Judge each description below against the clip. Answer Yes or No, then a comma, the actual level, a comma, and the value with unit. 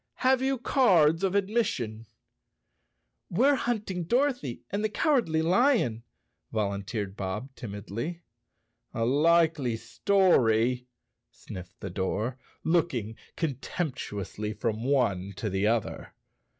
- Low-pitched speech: Yes, low, 130 Hz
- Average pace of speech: No, slow, 105 wpm